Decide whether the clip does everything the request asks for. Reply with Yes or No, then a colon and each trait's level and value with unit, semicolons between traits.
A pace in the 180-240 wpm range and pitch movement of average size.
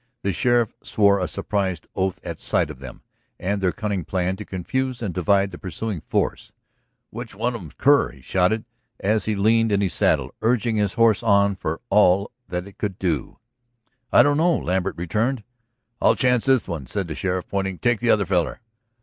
Yes: average, 190 wpm; average, 3.4 semitones